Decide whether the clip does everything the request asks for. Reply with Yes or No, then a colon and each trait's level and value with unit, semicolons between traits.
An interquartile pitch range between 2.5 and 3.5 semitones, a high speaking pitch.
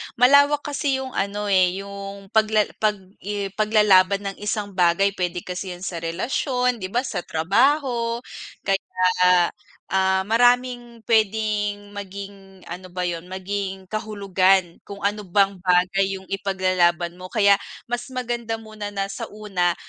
Yes: average, 2.8 semitones; high, 200 Hz